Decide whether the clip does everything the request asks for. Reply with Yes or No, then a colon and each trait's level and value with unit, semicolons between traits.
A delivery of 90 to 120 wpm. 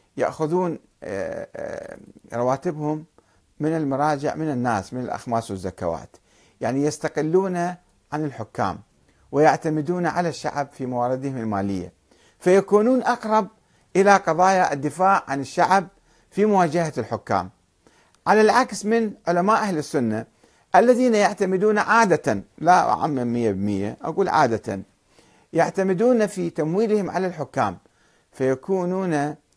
Yes: average, 100 wpm